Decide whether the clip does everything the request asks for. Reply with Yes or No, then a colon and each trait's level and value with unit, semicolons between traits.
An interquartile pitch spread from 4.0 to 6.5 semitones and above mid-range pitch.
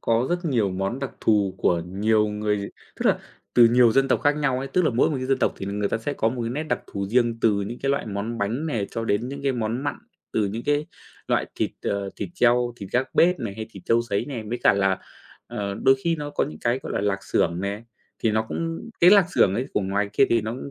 No: average, 4.8 semitones; low, 115 Hz